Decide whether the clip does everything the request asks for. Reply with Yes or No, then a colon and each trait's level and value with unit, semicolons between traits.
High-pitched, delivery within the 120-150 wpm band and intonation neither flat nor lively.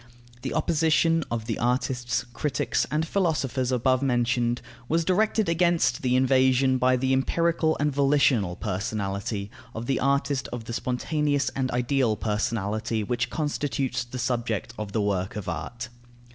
No: low, 125 Hz; average, 145 wpm; average, 3.5 semitones